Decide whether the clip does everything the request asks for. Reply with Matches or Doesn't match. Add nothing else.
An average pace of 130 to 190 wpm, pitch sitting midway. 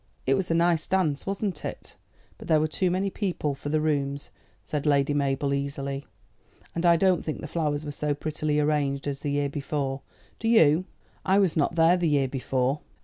Doesn't match